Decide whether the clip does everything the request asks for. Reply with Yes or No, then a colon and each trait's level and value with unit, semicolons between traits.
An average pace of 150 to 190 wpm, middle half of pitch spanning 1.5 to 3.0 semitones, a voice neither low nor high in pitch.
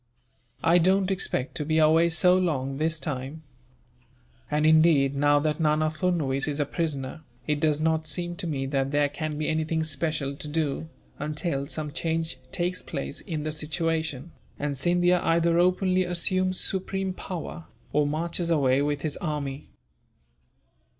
Yes: average, 155 wpm; narrow, 2.6 semitones; medium, 155 Hz